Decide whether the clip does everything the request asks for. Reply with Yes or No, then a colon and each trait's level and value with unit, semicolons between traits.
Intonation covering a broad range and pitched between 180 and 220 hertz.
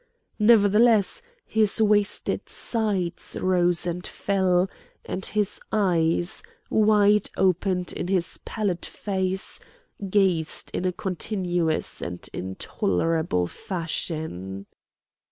No: average, 3.4 semitones; medium, 185 Hz